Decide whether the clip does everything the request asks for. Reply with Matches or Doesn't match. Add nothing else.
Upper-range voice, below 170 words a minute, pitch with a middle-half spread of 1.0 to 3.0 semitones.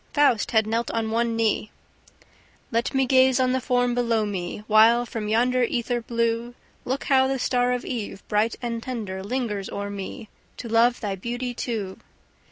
Doesn't match